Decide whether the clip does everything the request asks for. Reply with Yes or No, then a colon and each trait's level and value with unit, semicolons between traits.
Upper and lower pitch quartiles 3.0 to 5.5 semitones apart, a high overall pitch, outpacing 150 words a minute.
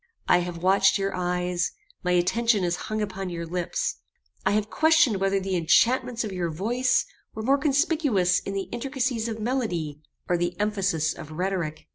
Yes: average, 4.6 semitones; high, 195 Hz; average, 170 wpm